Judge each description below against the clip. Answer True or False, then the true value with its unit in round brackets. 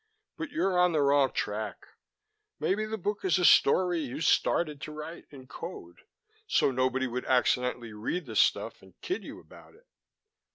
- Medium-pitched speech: True (150 Hz)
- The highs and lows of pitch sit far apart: True (6.2 semitones)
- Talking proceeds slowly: False (170 wpm)